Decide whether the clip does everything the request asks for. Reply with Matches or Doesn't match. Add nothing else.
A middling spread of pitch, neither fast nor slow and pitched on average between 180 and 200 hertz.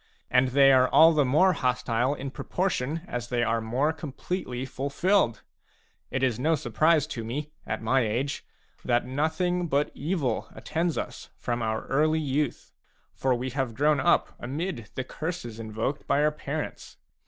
Doesn't match